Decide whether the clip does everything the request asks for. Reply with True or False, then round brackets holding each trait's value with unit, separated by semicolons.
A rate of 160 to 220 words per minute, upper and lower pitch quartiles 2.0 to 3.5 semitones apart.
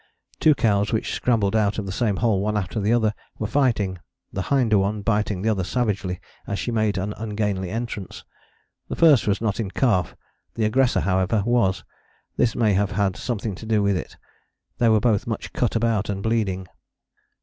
True (190 wpm; 2.6 semitones)